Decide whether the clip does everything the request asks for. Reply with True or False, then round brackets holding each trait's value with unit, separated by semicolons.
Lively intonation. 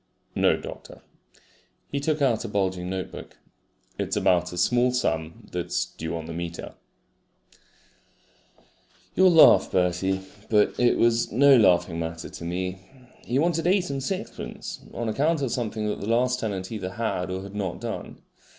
True (5.8 semitones)